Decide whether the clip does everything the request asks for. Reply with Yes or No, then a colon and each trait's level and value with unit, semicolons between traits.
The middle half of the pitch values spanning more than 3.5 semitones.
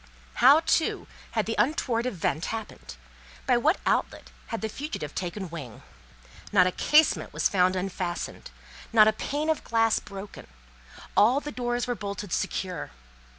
Yes: average, 4.9 semitones